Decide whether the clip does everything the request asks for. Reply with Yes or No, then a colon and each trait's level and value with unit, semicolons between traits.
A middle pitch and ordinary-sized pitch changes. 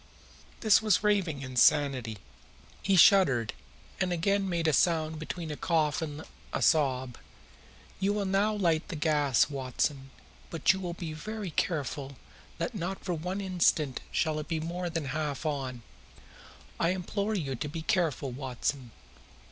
Yes: medium, 160 Hz; average, 4.7 semitones